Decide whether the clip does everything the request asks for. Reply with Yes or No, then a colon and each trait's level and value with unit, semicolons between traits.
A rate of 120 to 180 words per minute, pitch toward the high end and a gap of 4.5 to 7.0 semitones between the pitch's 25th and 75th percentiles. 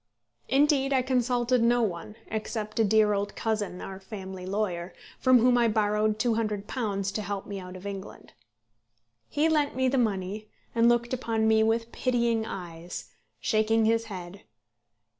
No: average, 155 wpm; high, 220 Hz; average, 3.0 semitones